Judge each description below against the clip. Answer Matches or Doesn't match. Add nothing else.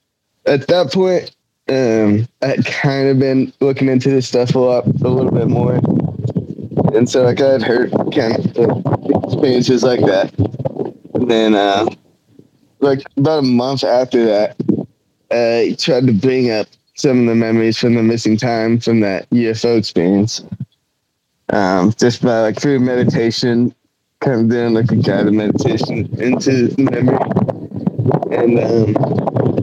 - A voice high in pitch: Doesn't match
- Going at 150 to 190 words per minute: Matches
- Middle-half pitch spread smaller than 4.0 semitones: Matches